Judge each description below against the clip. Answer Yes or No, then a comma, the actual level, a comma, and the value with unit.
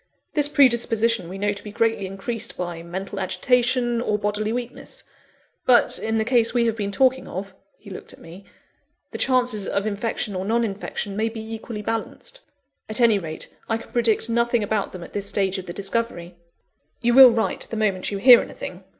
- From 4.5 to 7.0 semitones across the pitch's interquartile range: No, average, 3.1 semitones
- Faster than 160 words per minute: Yes, average, 195 wpm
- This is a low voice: No, high, 220 Hz